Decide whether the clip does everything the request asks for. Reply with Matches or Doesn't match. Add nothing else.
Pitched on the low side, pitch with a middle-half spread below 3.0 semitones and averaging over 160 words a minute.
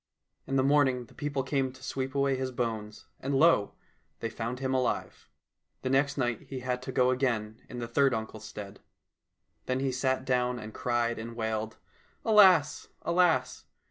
Matches